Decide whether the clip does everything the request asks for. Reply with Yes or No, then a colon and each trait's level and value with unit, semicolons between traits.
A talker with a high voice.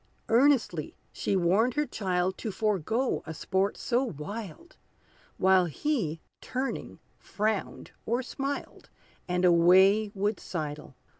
Yes: high, 200 Hz